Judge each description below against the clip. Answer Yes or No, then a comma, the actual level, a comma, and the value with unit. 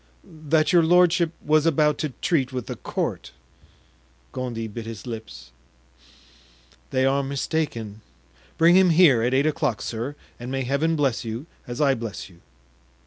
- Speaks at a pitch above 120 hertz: Yes, low, 135 Hz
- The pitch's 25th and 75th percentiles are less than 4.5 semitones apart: No, average, 5.2 semitones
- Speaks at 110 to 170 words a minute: Yes, average, 150 wpm